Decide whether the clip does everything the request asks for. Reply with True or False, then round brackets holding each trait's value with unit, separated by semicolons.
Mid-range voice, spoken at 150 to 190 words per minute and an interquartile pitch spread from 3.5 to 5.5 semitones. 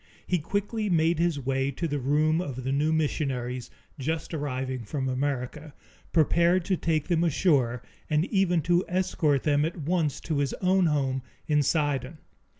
True (150 Hz; 160 wpm; 3.9 semitones)